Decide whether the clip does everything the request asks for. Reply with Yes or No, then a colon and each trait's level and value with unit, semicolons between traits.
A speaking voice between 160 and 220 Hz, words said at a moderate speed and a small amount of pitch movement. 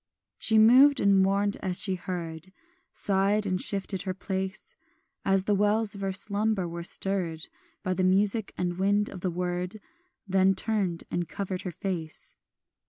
Yes: high, 190 Hz; average, 160 wpm; narrow, 2.0 semitones